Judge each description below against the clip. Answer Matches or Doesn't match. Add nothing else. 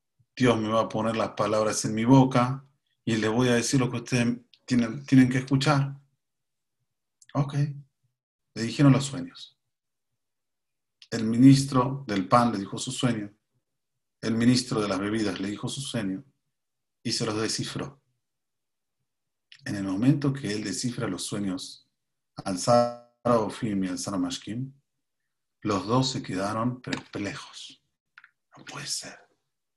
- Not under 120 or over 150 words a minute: Matches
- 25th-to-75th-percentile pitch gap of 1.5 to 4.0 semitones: Matches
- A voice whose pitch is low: Matches